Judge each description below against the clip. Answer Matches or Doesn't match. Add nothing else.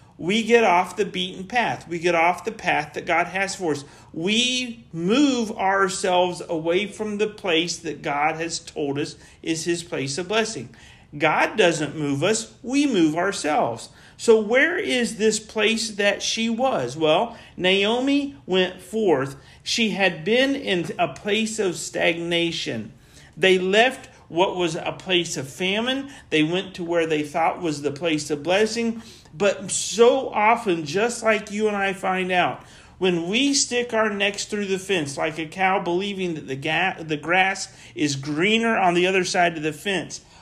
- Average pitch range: Matches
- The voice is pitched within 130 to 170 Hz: Doesn't match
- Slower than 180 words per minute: Matches